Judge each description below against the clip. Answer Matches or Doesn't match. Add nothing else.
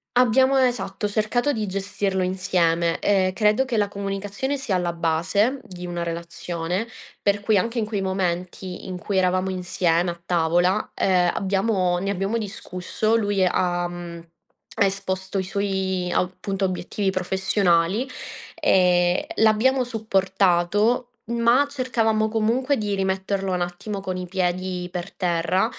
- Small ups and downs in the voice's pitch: Doesn't match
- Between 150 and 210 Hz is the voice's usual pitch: Matches